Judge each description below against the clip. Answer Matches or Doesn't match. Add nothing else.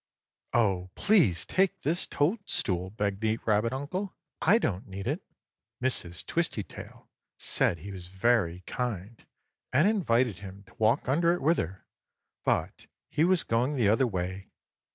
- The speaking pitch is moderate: Doesn't match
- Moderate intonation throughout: Doesn't match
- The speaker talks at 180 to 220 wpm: Doesn't match